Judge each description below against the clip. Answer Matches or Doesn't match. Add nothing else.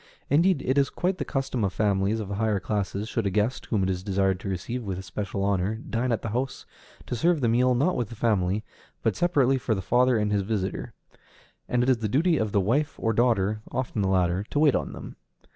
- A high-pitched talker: Doesn't match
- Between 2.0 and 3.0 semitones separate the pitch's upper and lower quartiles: Doesn't match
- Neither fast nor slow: Doesn't match